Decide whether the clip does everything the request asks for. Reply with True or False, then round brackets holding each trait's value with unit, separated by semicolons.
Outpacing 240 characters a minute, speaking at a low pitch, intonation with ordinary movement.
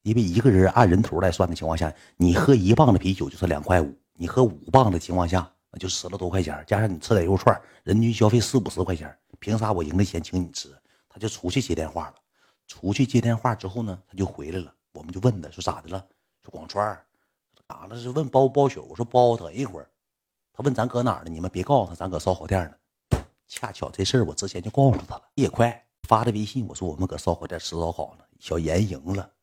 True (345 characters per minute; 95 Hz; 5.0 semitones)